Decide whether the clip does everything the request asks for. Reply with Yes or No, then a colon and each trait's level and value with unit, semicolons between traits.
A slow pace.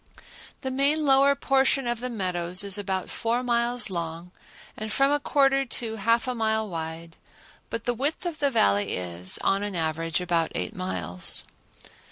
No: average, 170 wpm